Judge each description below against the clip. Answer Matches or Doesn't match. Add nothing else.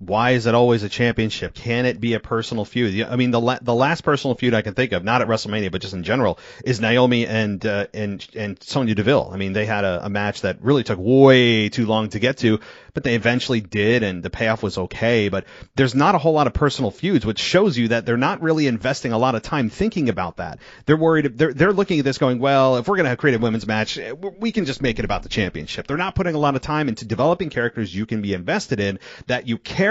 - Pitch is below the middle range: Matches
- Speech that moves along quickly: Matches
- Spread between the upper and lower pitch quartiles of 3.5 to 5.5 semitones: Matches